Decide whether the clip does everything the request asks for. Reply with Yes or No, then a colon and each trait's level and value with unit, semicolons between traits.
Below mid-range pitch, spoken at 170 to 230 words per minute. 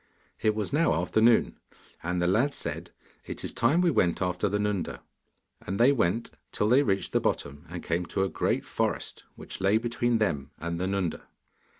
Yes: low, 100 Hz; average, 190 wpm